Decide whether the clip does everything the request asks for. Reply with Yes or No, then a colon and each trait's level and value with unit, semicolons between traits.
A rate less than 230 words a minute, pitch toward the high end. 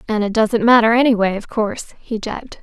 Yes: fast, 205 wpm; high, 220 Hz